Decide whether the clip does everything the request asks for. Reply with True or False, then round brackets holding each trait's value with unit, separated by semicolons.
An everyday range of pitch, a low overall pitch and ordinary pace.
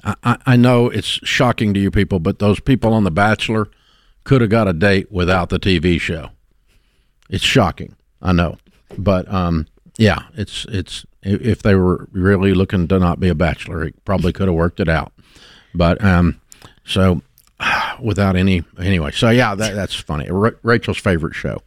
True (3.2 semitones; 95 Hz; 175 wpm)